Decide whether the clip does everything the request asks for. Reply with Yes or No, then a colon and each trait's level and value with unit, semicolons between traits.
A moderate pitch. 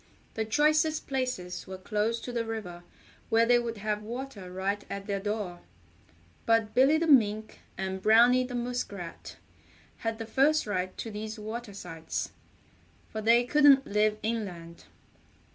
No: high, 220 Hz